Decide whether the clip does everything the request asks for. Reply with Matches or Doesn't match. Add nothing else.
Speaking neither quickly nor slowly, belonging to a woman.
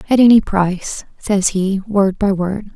Matches